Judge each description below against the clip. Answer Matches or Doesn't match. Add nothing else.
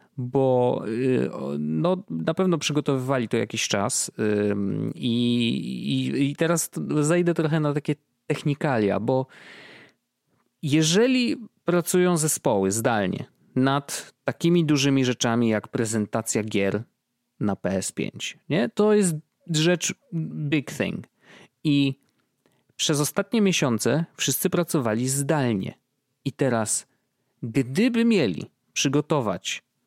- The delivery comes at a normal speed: Doesn't match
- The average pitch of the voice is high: Doesn't match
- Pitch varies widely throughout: Matches